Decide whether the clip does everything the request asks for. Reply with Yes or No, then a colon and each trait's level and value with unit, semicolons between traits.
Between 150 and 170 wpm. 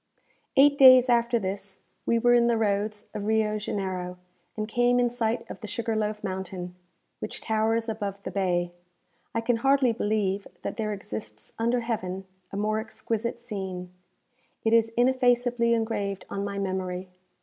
Yes: average, 160 wpm